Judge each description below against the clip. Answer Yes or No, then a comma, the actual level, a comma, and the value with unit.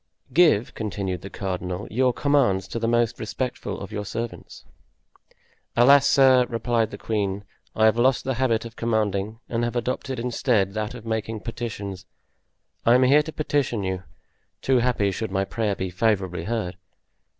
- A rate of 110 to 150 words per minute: No, average, 160 wpm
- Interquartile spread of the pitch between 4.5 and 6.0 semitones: No, average, 3.7 semitones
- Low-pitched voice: Yes, low, 115 Hz